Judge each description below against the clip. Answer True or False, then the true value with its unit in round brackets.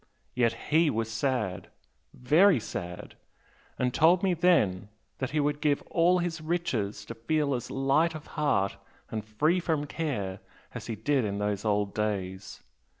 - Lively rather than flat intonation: True (6.8 semitones)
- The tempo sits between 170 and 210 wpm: False (155 wpm)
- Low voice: True (130 Hz)